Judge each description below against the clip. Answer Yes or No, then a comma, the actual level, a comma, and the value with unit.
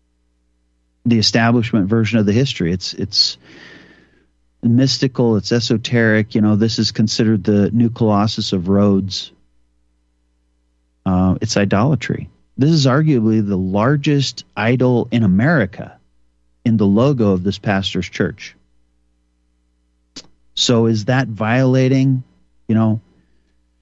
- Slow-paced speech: Yes, slow, 115 wpm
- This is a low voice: Yes, low, 105 Hz